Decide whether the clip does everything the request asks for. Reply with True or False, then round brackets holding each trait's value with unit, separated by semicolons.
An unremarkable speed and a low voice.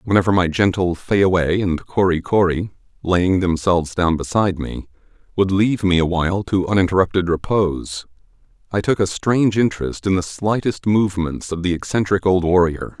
True (150 wpm; 95 Hz)